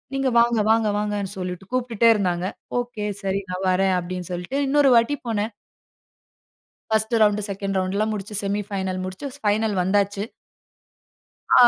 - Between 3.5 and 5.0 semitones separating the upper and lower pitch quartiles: No, average, 2.8 semitones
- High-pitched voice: Yes, high, 205 Hz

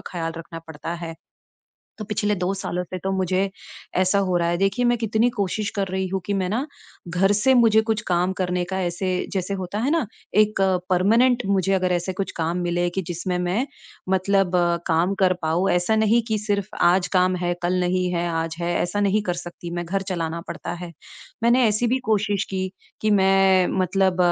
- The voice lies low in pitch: No, high, 190 Hz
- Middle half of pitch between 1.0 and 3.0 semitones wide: Yes, narrow, 2.6 semitones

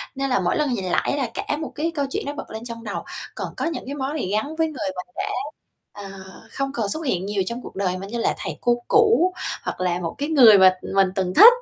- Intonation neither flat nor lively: No, wide, 6.9 semitones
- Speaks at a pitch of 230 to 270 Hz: Yes, high, 235 Hz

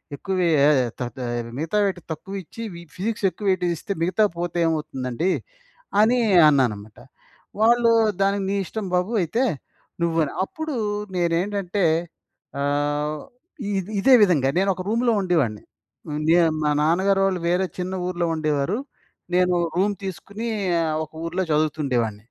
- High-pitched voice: No, medium, 175 Hz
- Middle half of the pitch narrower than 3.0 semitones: No, average, 4.6 semitones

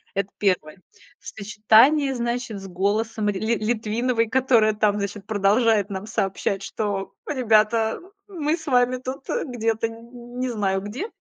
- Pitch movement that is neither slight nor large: Yes, average, 3.2 semitones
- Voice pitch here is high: Yes, high, 220 Hz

